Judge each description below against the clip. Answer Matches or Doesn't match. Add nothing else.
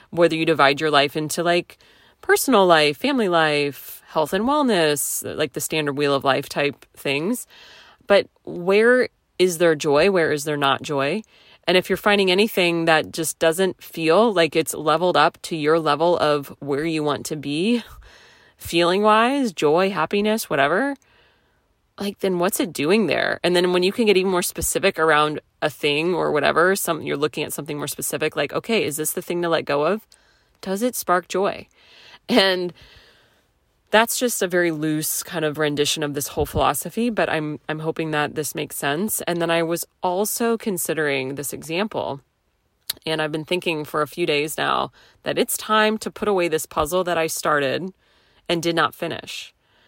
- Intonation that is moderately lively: Matches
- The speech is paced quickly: Doesn't match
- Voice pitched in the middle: Matches